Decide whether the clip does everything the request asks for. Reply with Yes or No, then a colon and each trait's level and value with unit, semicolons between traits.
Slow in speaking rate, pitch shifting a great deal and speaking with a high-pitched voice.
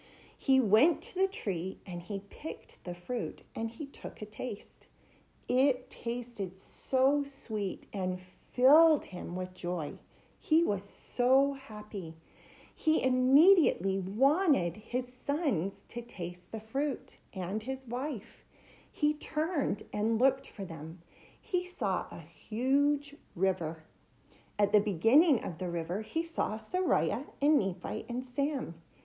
Yes: slow, 130 wpm; wide, 6.7 semitones; high, 245 Hz